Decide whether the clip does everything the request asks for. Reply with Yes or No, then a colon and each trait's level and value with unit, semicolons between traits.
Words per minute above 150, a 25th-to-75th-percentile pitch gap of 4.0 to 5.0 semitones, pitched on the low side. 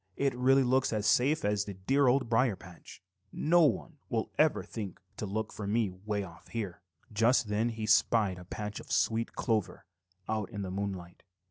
No: average, 190 wpm; average, 3.5 semitones; low, 110 Hz